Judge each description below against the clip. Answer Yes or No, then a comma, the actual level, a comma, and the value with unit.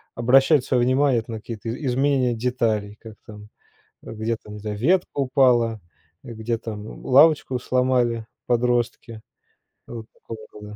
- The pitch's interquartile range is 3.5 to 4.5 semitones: No, narrow, 2.5 semitones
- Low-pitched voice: Yes, low, 120 Hz